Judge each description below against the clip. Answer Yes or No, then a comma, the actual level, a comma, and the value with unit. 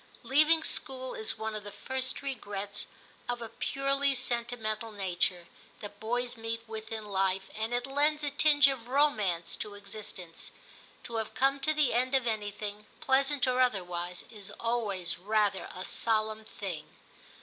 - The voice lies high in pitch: Yes, high, 225 Hz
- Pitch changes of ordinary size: Yes, average, 4.3 semitones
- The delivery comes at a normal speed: Yes, average, 155 wpm